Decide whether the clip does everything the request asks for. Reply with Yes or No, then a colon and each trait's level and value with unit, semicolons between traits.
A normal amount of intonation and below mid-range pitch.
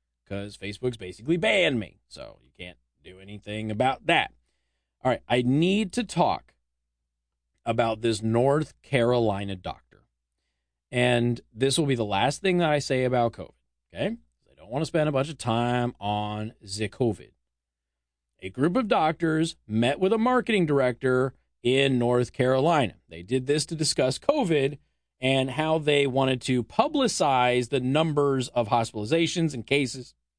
No: wide, 6.9 semitones; low, 125 Hz